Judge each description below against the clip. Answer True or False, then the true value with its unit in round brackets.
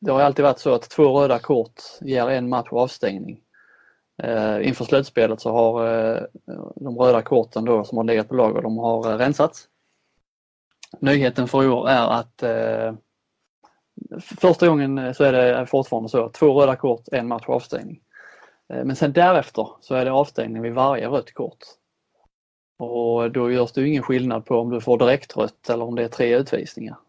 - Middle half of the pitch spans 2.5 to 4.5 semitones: True (2.8 semitones)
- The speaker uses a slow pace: False (175 wpm)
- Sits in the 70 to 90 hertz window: False (125 Hz)